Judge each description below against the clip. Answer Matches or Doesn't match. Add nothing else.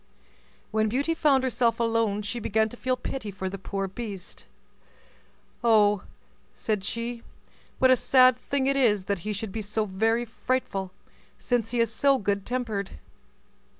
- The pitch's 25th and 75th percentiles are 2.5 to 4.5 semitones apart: Matches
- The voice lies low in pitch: Doesn't match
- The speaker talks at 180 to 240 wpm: Doesn't match